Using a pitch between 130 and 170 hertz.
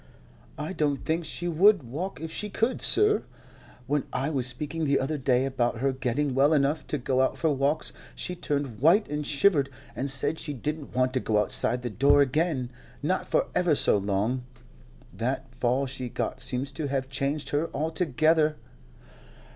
Yes: medium, 140 Hz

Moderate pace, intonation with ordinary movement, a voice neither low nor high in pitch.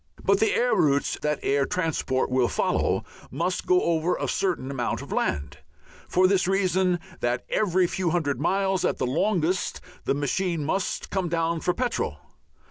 Yes: average, 165 wpm; average, 4.7 semitones; medium, 175 Hz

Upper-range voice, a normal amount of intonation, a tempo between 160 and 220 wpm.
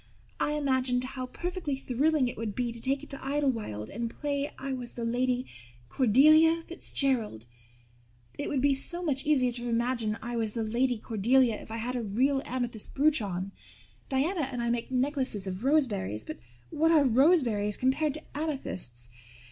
Yes: very high, 255 Hz; average, 3.6 semitones; average, 170 wpm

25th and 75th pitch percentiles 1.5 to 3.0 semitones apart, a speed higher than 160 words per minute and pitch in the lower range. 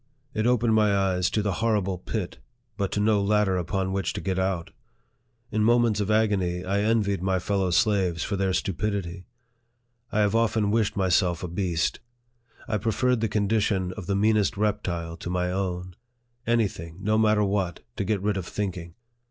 Yes: average, 2.7 semitones; average, 180 wpm; low, 100 Hz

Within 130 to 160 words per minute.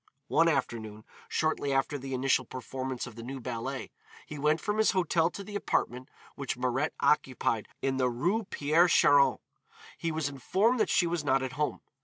No: average, 180 wpm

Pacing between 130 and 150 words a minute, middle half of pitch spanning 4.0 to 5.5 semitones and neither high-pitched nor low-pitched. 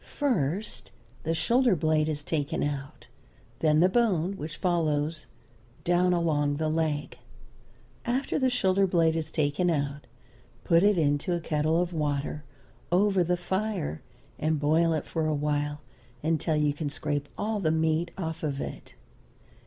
No: average, 145 wpm; average, 3.1 semitones; medium, 160 Hz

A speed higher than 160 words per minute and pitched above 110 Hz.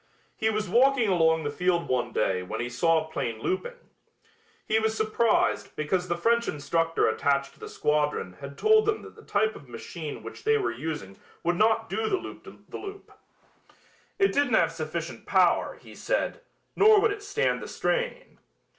Yes: average, 180 wpm; medium, 185 Hz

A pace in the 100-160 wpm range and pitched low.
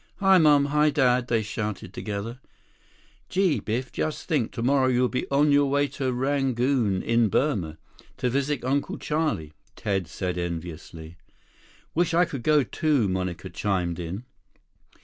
Yes: average, 150 wpm; low, 125 Hz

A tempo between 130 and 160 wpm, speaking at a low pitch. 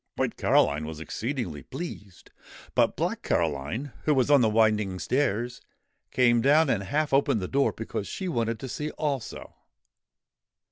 Yes: average, 150 wpm; low, 120 Hz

